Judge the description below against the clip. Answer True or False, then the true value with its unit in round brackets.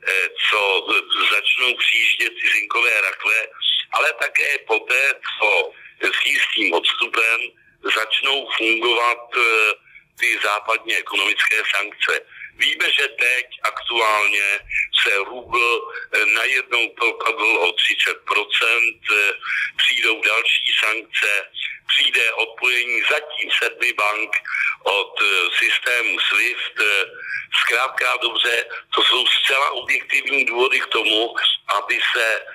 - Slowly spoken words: True (95 wpm)